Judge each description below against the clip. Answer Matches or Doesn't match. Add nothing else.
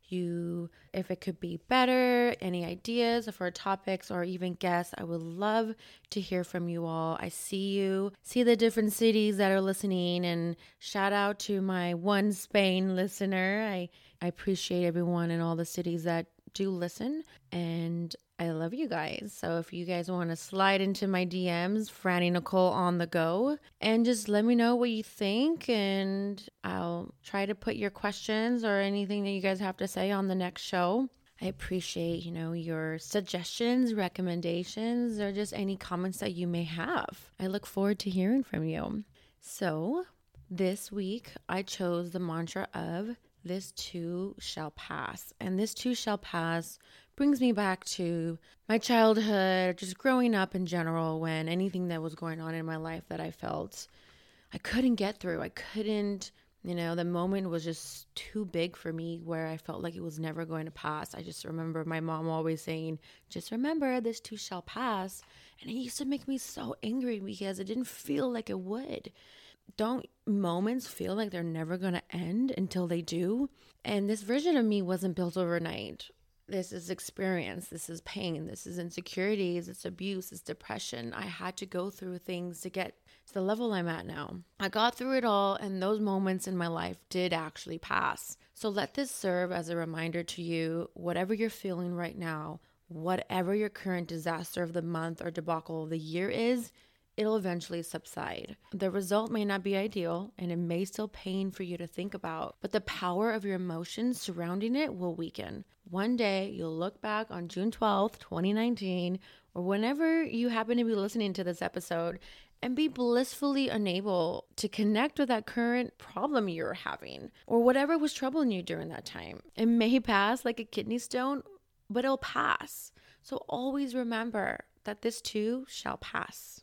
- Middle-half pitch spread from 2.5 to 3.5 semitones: Doesn't match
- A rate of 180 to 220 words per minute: Matches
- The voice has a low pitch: Doesn't match